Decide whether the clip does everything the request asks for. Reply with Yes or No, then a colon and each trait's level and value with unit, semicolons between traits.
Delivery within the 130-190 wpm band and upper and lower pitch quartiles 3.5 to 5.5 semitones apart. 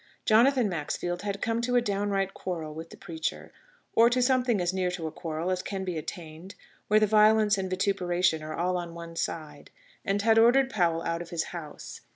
No: average, 200 wpm; average, 4.2 semitones